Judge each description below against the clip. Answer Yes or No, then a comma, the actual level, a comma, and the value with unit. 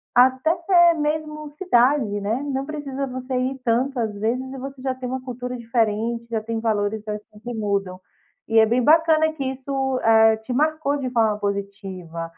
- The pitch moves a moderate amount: Yes, average, 3.9 semitones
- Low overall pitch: No, very high, 250 Hz